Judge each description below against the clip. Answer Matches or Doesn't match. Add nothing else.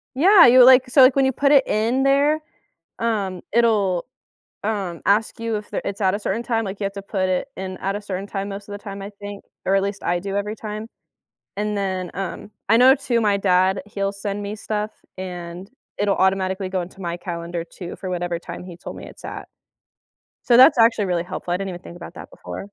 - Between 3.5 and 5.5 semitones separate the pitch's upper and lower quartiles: Doesn't match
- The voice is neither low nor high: Doesn't match